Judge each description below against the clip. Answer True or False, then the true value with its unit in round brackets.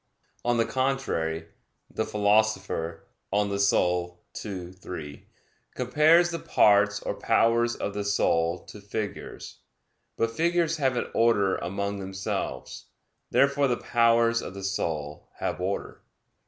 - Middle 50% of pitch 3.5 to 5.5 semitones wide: True (4.4 semitones)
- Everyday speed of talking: False (125 wpm)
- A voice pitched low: True (100 Hz)